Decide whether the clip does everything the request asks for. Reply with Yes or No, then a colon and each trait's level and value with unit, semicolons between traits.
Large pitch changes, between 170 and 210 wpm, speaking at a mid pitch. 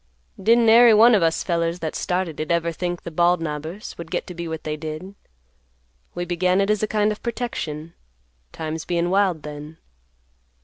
No: average, 3.6 semitones; average, 185 wpm; medium, 175 Hz